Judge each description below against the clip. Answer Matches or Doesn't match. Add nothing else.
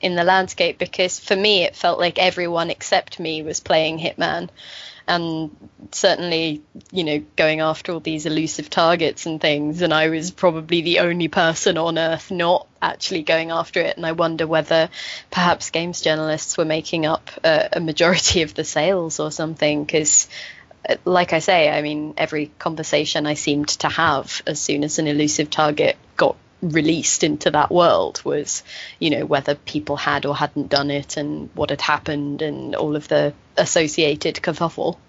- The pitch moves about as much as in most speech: Doesn't match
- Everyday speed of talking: Matches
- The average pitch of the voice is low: Doesn't match